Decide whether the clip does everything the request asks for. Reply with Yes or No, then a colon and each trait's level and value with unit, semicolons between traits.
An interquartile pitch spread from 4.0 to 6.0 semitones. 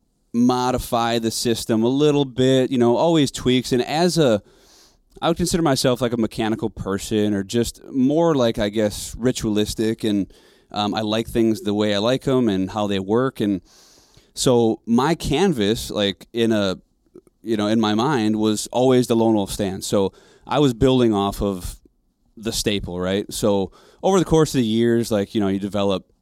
No: average, 3.5 semitones